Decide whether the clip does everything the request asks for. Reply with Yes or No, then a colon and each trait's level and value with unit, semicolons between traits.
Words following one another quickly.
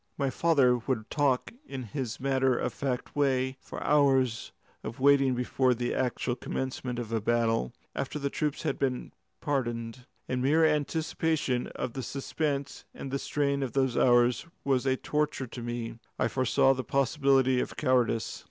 No: average, 165 wpm